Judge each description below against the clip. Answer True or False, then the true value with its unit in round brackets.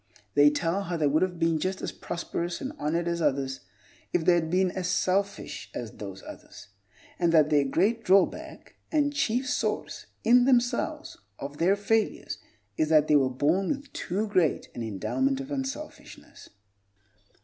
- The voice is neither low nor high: True (175 Hz)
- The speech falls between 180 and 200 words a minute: False (170 wpm)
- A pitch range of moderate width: False (6.7 semitones)